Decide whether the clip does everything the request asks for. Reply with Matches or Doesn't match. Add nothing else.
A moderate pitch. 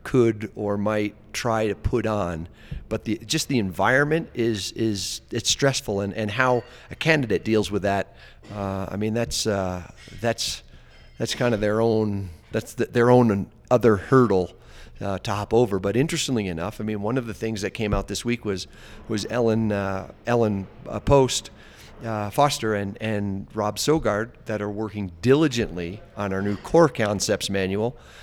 Doesn't match